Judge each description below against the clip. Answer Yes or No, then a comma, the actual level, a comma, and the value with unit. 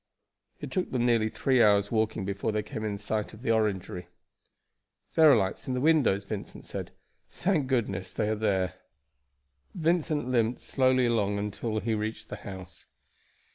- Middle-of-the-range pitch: No, low, 110 Hz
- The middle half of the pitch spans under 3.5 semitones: No, average, 3.9 semitones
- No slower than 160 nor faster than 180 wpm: Yes, average, 165 wpm